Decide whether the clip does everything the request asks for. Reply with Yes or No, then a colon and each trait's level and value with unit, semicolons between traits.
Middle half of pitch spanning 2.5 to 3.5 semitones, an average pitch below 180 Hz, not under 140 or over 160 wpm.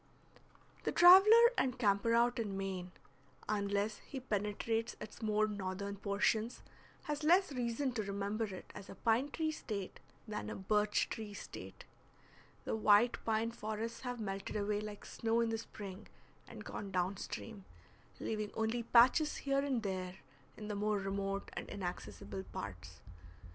No: average, 2.8 semitones; high, 215 Hz; average, 150 wpm